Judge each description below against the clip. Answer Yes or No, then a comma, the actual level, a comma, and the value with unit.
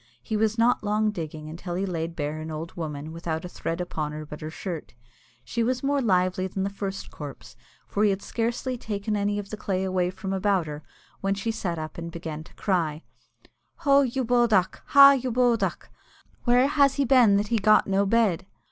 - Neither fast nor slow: No, fast, 210 wpm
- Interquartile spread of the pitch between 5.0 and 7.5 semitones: Yes, wide, 5.4 semitones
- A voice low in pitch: No, high, 195 Hz